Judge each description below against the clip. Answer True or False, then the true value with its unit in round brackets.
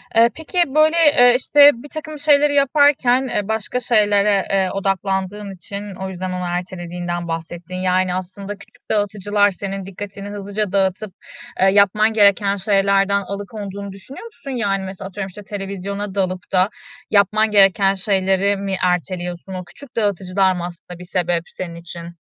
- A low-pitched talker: False (195 Hz)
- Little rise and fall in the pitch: True (2.2 semitones)